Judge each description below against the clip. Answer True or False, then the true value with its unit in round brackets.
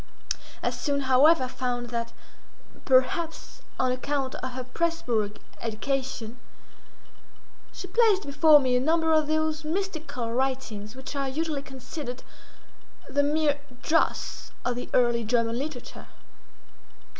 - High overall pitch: True (270 Hz)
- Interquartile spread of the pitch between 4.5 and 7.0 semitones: False (4.0 semitones)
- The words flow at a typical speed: False (120 wpm)